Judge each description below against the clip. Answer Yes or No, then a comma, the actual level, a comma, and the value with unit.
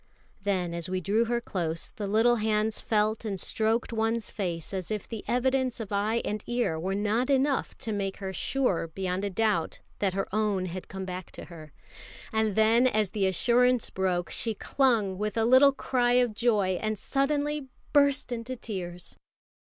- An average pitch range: Yes, average, 4.0 semitones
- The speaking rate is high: No, average, 180 wpm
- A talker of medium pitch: No, high, 215 Hz